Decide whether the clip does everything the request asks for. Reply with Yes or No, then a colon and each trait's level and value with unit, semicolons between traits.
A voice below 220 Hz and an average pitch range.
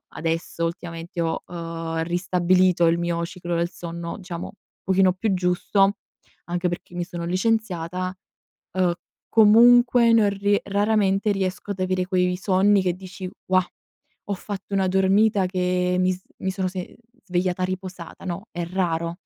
No: medium, 185 Hz; narrow, 2.1 semitones